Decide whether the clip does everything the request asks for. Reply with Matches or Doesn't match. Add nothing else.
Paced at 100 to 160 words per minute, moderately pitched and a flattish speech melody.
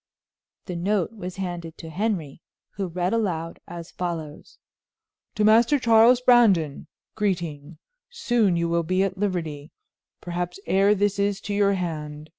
Doesn't match